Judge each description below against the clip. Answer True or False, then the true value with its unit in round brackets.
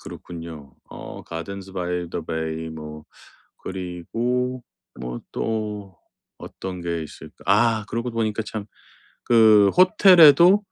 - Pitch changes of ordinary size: False (5.7 semitones)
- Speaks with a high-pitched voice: False (100 Hz)